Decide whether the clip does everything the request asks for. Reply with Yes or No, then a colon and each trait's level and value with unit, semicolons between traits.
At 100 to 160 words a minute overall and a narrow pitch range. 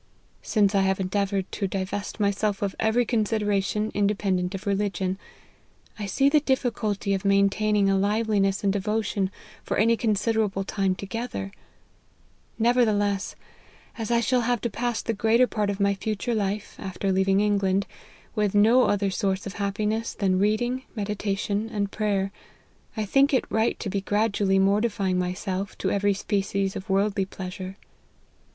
Yes: average, 150 wpm; narrow, 1.9 semitones